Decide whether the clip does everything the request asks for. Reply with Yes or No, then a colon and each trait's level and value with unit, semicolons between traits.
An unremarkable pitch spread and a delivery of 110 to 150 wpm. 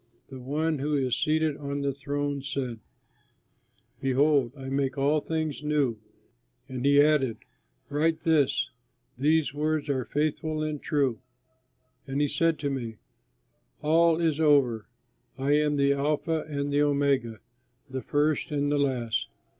No: narrow, 2.2 semitones; average, 140 wpm